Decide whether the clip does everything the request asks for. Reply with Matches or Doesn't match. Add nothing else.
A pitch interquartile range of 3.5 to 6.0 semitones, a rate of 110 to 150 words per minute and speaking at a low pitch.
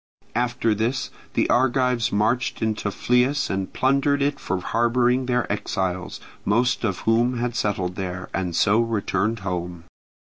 Matches